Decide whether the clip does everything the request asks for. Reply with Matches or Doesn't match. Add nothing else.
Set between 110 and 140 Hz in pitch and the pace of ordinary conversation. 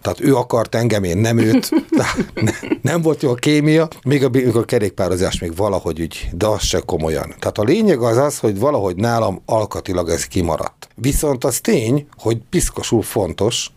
Doesn't match